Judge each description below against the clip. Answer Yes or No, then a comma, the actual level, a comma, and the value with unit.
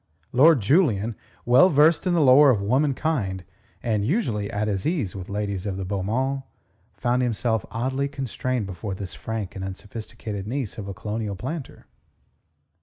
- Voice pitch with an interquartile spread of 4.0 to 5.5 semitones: Yes, average, 5.1 semitones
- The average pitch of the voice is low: Yes, low, 110 Hz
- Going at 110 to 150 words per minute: No, average, 160 wpm